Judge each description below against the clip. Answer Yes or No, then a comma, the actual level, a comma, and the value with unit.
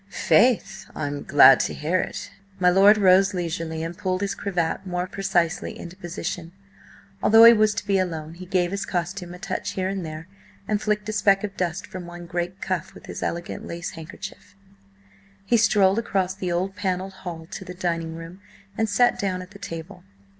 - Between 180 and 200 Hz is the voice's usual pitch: Yes, medium, 185 Hz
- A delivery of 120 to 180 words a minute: No, average, 190 wpm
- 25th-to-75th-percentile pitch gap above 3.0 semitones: No, narrow, 2.4 semitones